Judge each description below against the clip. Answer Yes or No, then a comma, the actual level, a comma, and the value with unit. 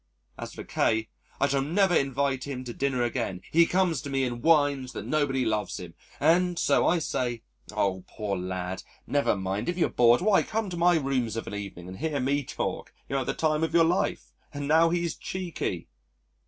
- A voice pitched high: No, medium, 140 Hz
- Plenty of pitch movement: Yes, wide, 6.2 semitones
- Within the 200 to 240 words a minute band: Yes, fast, 205 wpm